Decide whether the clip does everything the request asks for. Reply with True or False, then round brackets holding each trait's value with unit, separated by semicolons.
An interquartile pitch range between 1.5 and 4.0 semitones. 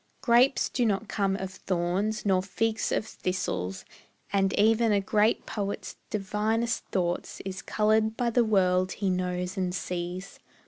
True (2.9 semitones)